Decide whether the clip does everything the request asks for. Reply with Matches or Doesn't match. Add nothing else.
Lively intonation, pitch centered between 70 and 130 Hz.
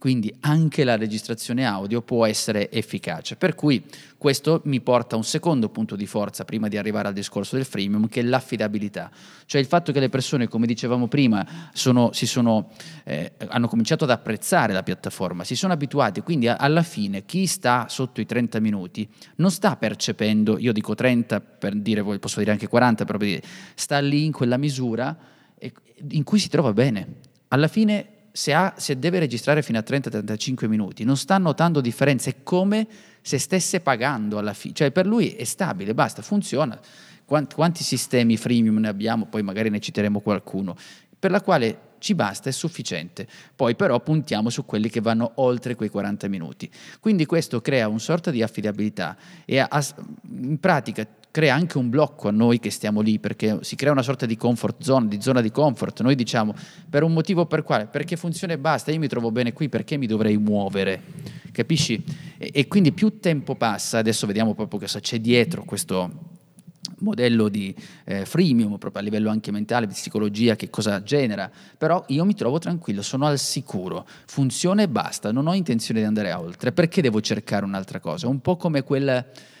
Matches